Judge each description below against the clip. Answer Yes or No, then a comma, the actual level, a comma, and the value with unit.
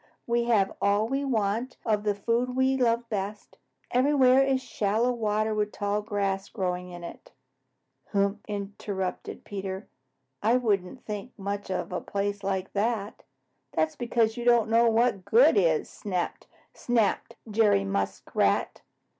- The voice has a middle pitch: No, high, 210 Hz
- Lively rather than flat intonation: No, average, 3.2 semitones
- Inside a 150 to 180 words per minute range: No, average, 140 wpm